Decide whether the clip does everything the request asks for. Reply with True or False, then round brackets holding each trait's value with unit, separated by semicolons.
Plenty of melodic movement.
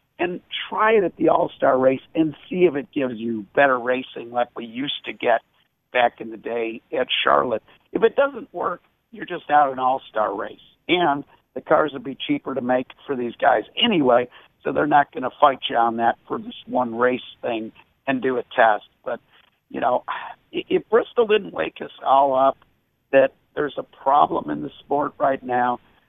True (5.8 semitones)